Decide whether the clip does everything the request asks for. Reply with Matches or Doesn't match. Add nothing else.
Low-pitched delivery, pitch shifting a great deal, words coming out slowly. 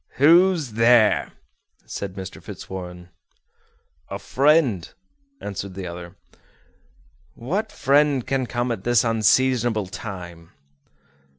Matches